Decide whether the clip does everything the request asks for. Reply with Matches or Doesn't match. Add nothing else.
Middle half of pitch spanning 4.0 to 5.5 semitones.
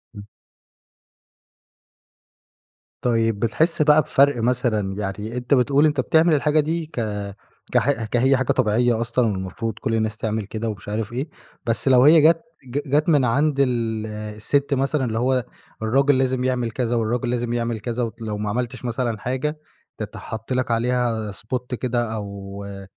Doesn't match